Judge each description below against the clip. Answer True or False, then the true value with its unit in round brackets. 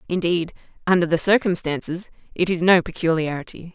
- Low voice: False (175 Hz)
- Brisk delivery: False (130 wpm)